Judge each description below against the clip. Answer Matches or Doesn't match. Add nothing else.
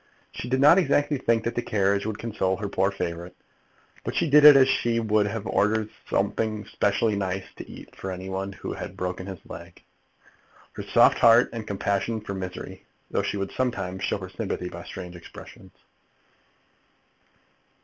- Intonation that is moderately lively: Matches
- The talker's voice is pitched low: Matches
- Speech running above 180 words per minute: Doesn't match